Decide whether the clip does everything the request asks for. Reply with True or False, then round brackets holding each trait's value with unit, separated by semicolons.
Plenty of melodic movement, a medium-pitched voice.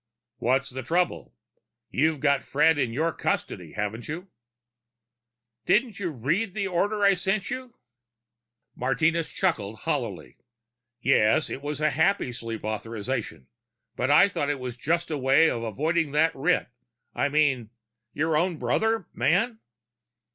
True (5.8 semitones; 150 Hz)